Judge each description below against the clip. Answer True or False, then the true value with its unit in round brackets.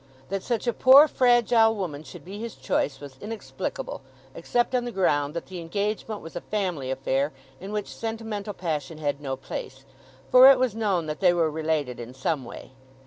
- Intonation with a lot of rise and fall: True (7.3 semitones)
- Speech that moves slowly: False (190 wpm)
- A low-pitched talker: False (185 Hz)